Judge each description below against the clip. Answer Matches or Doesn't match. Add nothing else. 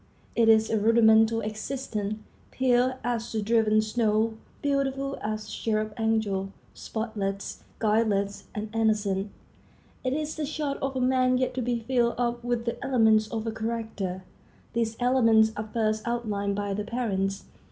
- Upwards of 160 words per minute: Doesn't match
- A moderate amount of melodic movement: Doesn't match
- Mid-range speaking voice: Doesn't match